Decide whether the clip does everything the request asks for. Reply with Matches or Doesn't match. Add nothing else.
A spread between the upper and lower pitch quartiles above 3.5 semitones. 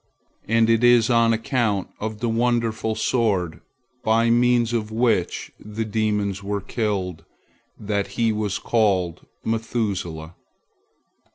Doesn't match